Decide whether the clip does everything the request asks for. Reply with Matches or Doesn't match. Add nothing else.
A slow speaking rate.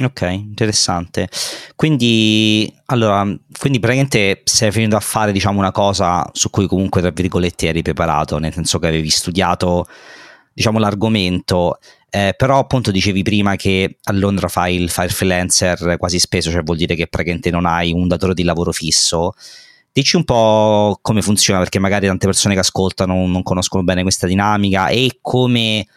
Doesn't match